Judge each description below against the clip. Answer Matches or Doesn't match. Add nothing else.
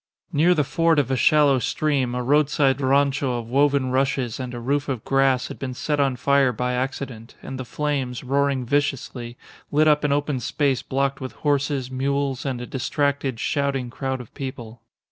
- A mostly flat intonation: Matches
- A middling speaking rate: Matches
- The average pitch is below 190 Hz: Matches